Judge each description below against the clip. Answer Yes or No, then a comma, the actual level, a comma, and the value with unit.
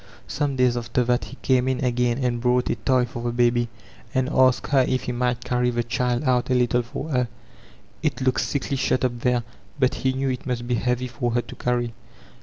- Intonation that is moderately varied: No, narrow, 1.2 semitones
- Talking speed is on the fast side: Yes, fast, 220 wpm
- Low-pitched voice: Yes, low, 125 Hz